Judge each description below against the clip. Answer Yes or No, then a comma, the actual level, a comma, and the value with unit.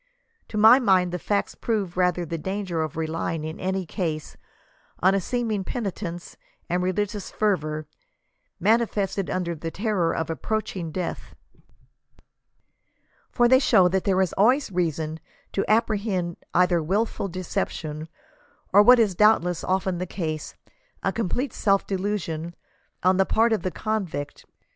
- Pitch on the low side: No, medium, 185 Hz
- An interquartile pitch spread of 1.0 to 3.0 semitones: No, average, 3.7 semitones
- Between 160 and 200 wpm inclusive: No, average, 145 wpm